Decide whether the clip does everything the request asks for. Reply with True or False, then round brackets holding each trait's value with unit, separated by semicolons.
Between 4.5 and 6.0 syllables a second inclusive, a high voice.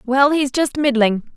False (4.1 syllables/s; 265 Hz)